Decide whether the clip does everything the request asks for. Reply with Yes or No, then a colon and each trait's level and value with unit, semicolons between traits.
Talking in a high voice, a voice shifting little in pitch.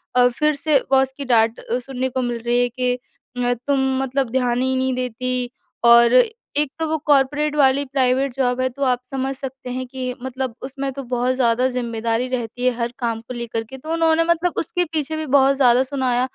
Yes: very high, 255 Hz; narrow, 1.8 semitones